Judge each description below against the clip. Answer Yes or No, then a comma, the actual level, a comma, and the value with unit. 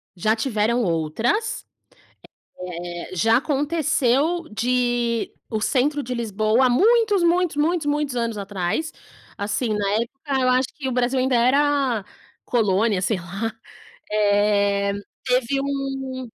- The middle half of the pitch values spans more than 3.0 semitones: Yes, average, 4.7 semitones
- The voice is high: Yes, high, 245 Hz